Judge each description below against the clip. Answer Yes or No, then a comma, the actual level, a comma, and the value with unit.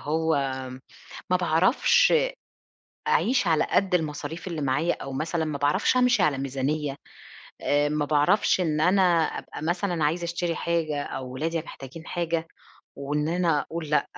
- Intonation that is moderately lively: Yes, average, 3.1 semitones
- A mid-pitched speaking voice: Yes, medium, 160 Hz